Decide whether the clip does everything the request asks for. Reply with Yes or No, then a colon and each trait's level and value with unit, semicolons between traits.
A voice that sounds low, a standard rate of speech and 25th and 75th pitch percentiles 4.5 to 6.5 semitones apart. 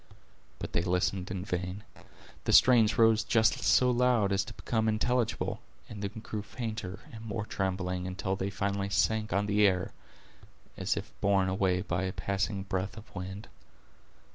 No: low, 100 Hz; average, 165 wpm; average, 2.7 semitones